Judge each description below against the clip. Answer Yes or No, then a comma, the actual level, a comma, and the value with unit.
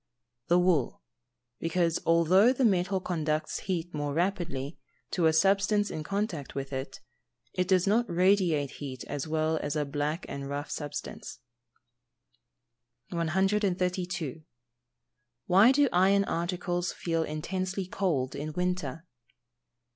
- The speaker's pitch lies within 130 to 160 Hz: No, medium, 175 Hz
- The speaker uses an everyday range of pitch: Yes, average, 3.7 semitones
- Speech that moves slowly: Yes, slow, 125 wpm